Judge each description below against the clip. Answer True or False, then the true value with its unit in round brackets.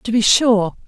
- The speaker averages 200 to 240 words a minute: True (205 wpm)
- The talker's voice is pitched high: True (220 Hz)